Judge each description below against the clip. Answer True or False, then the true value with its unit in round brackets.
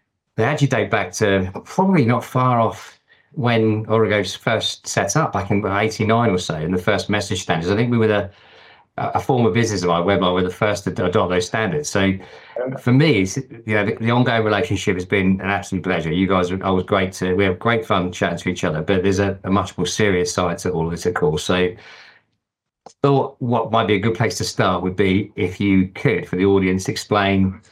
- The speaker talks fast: True (230 wpm)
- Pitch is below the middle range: True (100 Hz)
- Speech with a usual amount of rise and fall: True (3.5 semitones)